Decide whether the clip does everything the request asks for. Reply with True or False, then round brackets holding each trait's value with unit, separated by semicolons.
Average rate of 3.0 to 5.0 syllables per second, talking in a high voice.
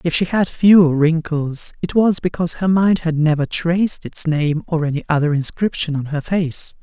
False (4.8 syllables/s; 165 Hz)